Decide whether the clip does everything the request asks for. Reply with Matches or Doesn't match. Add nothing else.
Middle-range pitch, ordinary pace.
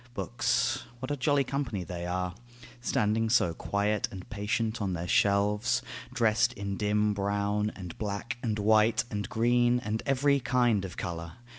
Doesn't match